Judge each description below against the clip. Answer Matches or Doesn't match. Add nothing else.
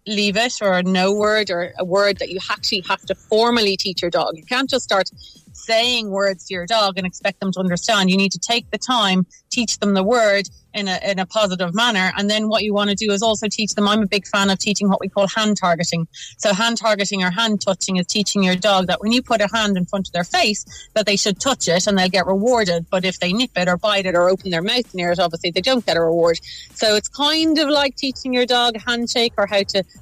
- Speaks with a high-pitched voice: Matches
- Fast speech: Matches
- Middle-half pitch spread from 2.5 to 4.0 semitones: Matches